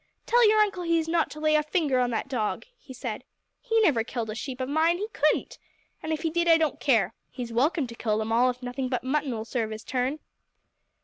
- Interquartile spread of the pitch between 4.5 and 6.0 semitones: Yes, average, 5.1 semitones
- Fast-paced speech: Yes, fast, 240 wpm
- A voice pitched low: No, very high, 270 Hz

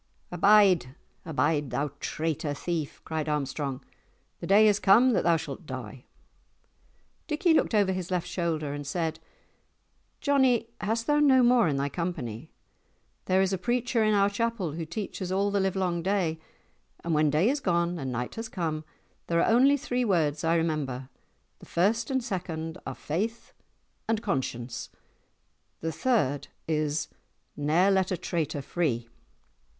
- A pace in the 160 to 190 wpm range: No, average, 150 wpm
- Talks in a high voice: No, medium, 175 Hz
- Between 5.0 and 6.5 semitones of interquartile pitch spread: Yes, wide, 5.5 semitones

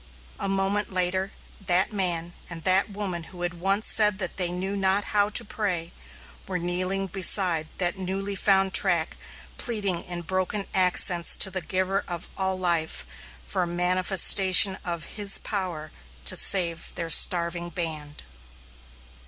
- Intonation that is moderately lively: No, narrow, 2.0 semitones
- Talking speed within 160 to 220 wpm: No, average, 145 wpm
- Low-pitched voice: No, medium, 185 Hz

